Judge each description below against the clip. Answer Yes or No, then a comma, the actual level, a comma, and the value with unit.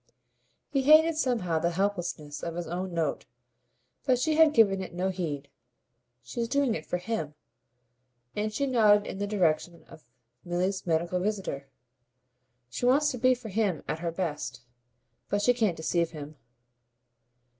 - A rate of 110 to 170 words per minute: Yes, average, 155 wpm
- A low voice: No, high, 190 Hz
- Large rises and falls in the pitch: Yes, wide, 5.7 semitones